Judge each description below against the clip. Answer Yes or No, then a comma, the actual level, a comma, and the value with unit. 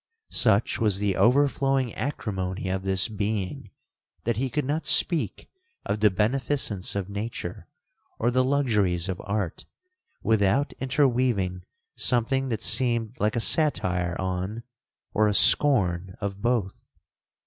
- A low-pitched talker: Yes, low, 110 Hz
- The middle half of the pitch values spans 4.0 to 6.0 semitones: Yes, average, 5.0 semitones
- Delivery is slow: Yes, slow, 130 wpm